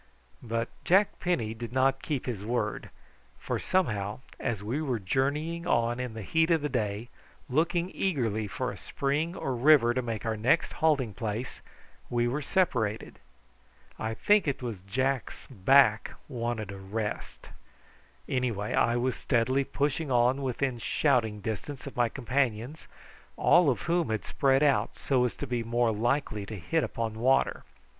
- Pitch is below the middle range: Yes, low, 125 Hz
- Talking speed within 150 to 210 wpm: Yes, average, 160 wpm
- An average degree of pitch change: Yes, average, 4.0 semitones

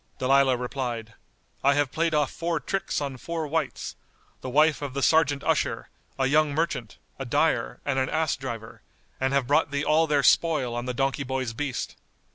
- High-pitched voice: No, medium, 140 Hz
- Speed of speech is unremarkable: Yes, average, 185 wpm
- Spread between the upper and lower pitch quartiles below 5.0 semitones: Yes, average, 2.9 semitones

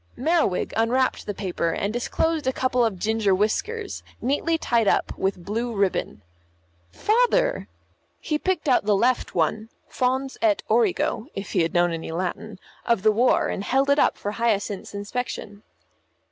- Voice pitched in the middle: No, high, 230 Hz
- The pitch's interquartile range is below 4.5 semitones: No, average, 5.1 semitones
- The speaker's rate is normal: Yes, average, 160 wpm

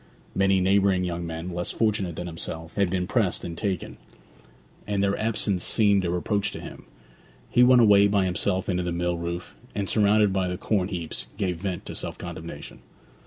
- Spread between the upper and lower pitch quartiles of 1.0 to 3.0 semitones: Yes, narrow, 2.6 semitones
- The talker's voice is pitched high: No, very low, 95 Hz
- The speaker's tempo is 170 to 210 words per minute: Yes, average, 185 wpm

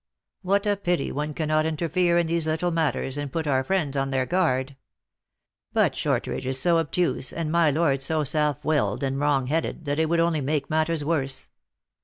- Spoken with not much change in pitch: No, average, 3.3 semitones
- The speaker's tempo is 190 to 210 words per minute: Yes, average, 195 wpm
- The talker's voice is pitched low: No, medium, 155 Hz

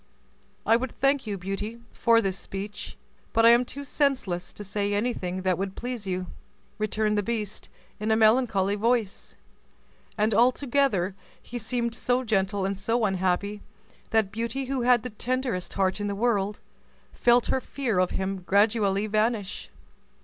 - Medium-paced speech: Yes, average, 155 wpm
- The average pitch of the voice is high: Yes, high, 215 Hz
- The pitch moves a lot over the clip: No, average, 3.5 semitones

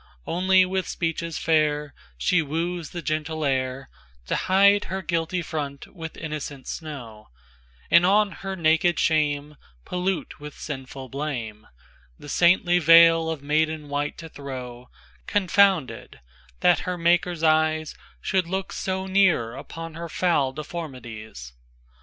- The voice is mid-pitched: Yes, medium, 155 Hz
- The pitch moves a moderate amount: Yes, average, 4.4 semitones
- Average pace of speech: No, slow, 110 wpm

